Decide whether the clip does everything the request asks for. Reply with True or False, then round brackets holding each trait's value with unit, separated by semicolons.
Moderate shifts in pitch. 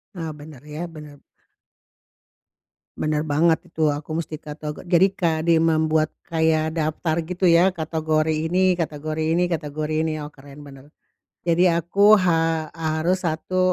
False (1.6 semitones)